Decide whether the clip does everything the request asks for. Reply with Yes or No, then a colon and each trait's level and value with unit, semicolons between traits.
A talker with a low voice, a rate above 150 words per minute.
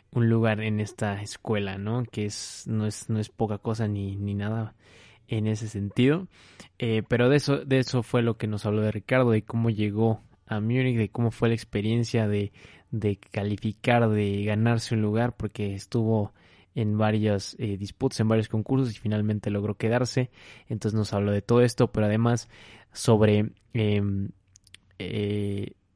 Yes: low, 110 Hz; average, 170 wpm